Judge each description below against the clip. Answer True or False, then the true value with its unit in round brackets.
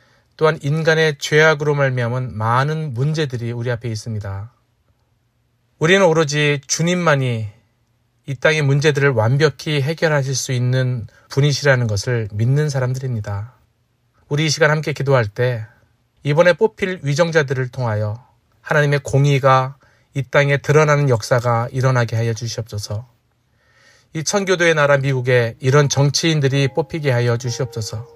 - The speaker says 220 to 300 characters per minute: False (315 characters per minute)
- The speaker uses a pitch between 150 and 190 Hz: False (130 Hz)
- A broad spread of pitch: False (3.9 semitones)